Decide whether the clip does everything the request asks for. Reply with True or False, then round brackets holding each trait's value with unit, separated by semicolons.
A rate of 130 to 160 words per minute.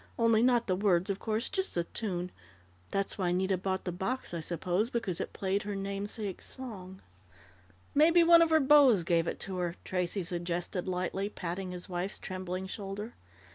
False (180 wpm)